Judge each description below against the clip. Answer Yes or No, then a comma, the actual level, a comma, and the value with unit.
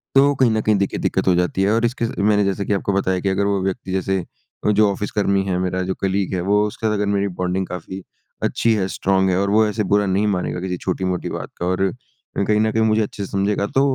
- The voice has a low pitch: Yes, low, 100 Hz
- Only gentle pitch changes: Yes, narrow, 1.9 semitones